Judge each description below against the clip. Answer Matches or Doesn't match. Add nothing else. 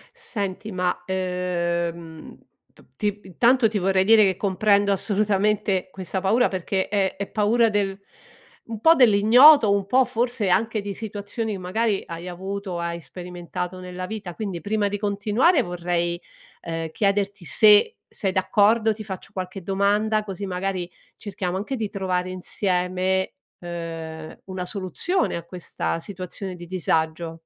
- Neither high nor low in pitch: Doesn't match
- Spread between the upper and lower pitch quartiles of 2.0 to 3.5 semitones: Matches